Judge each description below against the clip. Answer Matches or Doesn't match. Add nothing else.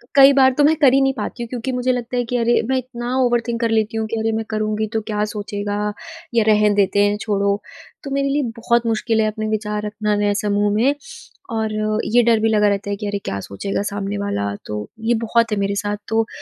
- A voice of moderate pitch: Doesn't match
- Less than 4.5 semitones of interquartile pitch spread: Matches